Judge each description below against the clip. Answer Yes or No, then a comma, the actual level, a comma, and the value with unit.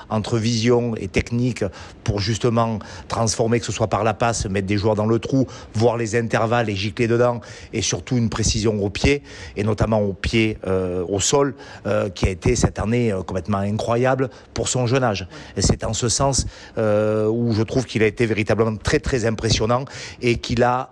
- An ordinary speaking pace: Yes, average, 200 wpm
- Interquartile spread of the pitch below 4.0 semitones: Yes, narrow, 2.4 semitones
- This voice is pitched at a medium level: No, low, 115 Hz